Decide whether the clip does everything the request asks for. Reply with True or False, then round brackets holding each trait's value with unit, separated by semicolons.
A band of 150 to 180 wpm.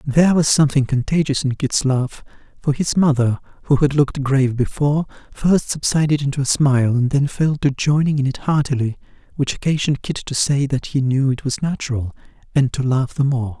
False (195 wpm)